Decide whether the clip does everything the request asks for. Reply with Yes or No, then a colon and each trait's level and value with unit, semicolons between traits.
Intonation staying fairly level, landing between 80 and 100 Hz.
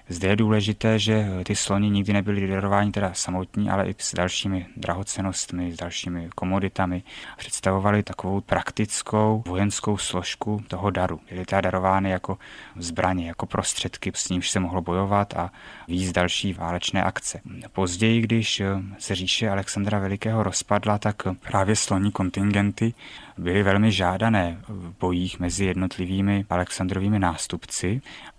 Yes: narrow, 2.2 semitones; very low, 95 Hz